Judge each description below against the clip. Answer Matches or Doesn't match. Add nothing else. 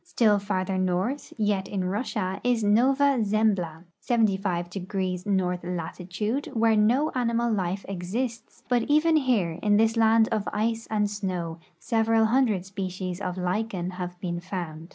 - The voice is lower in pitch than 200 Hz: Doesn't match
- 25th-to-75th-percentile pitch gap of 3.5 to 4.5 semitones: Matches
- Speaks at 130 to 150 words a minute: Matches